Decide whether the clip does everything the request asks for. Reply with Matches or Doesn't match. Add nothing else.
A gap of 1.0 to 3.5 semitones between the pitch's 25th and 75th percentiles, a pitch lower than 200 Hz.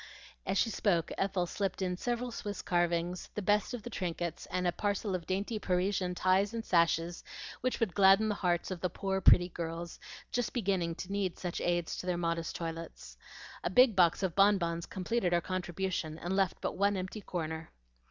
Matches